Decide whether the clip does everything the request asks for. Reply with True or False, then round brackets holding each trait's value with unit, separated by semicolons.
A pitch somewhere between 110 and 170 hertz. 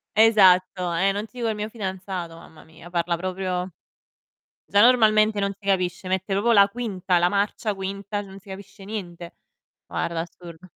False (195 Hz)